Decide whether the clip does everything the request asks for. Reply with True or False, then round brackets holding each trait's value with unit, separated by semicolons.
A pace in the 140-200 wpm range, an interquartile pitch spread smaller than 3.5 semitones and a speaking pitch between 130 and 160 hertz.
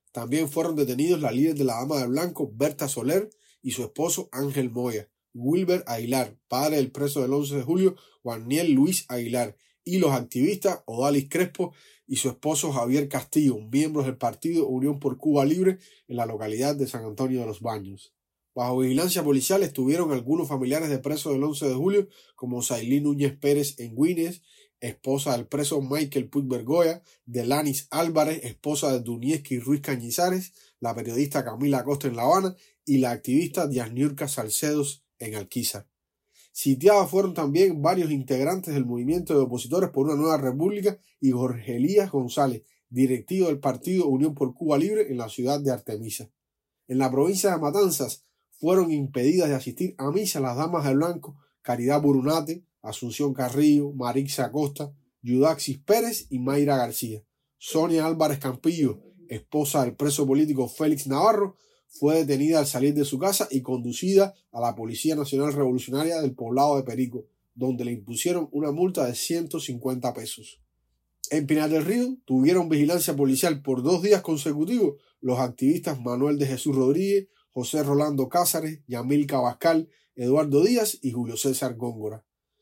False (160 wpm; 3.8 semitones; 140 Hz)